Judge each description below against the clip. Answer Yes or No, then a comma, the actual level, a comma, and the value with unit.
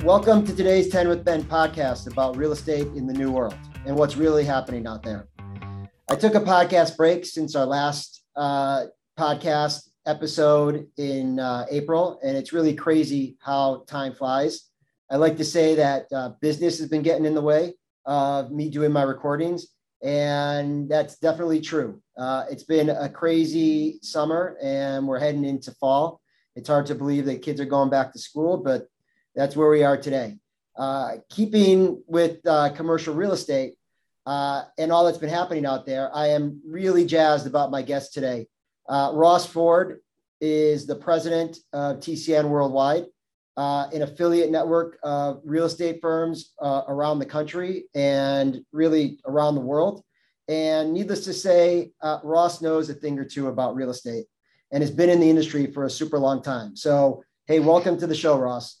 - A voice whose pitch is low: No, medium, 150 Hz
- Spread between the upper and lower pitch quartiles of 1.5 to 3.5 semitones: Yes, average, 3.0 semitones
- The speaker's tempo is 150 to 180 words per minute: Yes, average, 175 wpm